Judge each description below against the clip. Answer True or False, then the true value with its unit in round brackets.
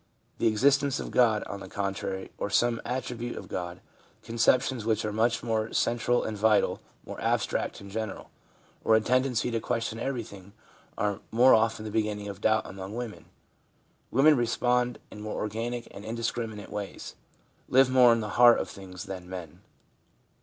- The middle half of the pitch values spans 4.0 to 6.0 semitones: False (2.7 semitones)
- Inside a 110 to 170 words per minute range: False (180 wpm)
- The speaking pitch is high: False (110 Hz)